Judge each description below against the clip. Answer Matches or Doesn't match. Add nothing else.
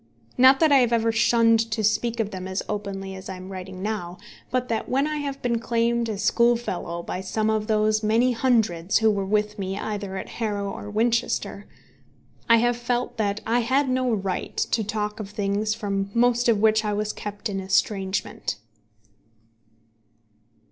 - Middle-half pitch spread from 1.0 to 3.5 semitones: Matches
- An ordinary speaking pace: Matches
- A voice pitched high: Matches